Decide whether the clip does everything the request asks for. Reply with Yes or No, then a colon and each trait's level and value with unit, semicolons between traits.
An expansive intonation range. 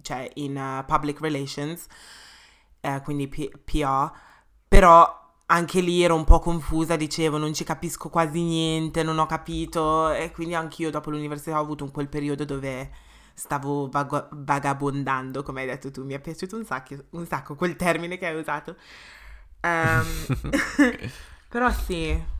No: average, 2.8 semitones